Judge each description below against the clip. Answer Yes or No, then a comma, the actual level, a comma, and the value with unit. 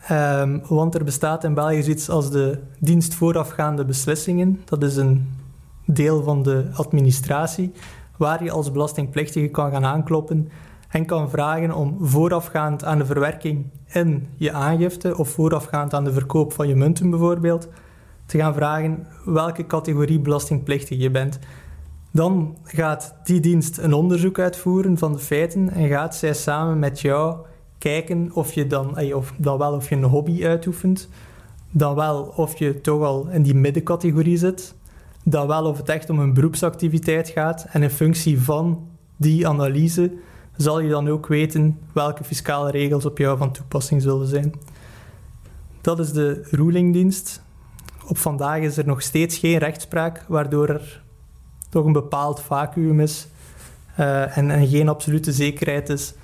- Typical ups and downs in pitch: No, narrow, 2.3 semitones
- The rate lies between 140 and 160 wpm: Yes, average, 155 wpm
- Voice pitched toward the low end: No, medium, 150 Hz